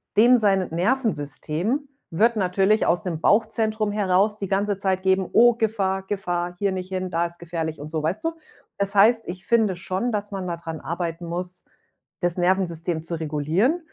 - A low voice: No, high, 190 Hz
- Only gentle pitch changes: No, average, 3.5 semitones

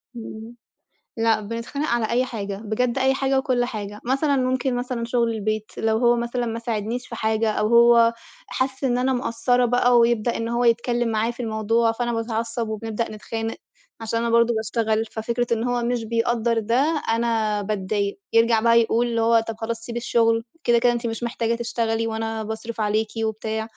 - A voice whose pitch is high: Yes, high, 230 Hz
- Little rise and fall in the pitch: Yes, narrow, 1.4 semitones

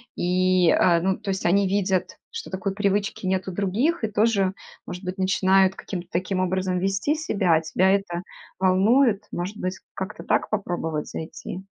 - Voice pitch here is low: No, high, 190 Hz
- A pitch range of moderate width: No, narrow, 1.6 semitones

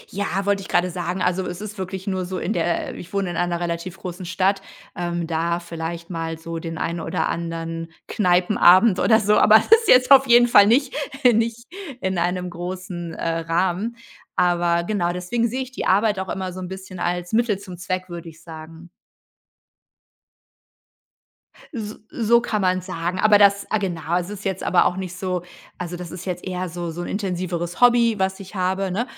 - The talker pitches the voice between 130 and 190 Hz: Yes, medium, 185 Hz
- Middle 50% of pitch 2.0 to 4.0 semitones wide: Yes, average, 2.8 semitones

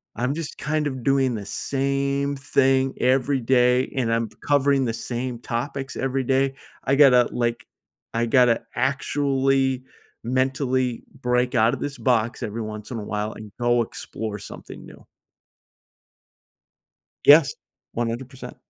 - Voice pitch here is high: No, low, 130 Hz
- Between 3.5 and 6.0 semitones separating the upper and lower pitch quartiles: No, narrow, 2.5 semitones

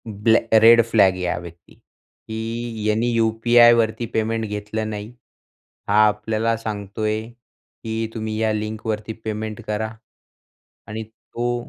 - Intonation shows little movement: Yes, narrow, 1.1 semitones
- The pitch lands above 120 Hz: No, low, 110 Hz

